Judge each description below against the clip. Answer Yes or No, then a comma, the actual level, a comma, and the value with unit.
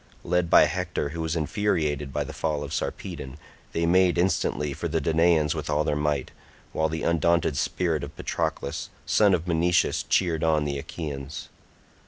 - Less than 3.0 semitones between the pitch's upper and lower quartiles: Yes, narrow, 2.5 semitones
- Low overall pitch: Yes, very low, 80 Hz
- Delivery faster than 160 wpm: Yes, average, 170 wpm